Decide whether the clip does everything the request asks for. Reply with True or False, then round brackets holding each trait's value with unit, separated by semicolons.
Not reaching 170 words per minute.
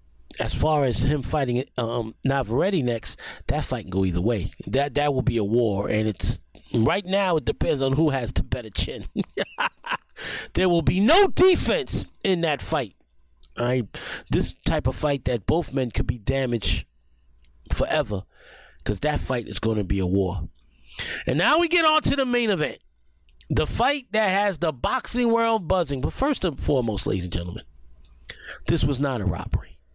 False (180 wpm)